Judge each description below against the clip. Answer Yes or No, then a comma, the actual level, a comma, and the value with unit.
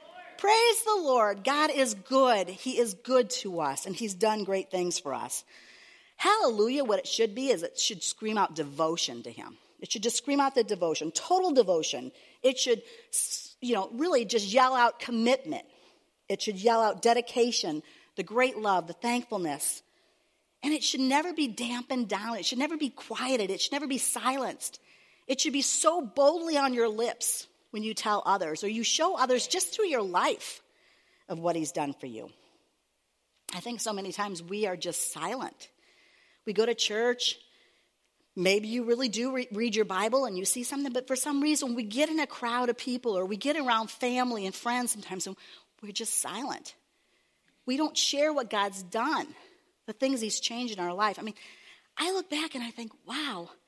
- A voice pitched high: Yes, high, 245 Hz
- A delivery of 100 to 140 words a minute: No, average, 190 wpm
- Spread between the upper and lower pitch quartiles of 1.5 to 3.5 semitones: No, average, 5.1 semitones